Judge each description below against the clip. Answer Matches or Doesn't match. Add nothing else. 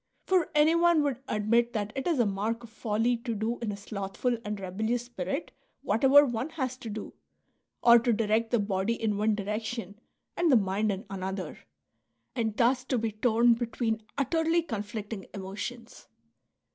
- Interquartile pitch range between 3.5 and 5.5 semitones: Doesn't match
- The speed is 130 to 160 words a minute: Doesn't match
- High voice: Matches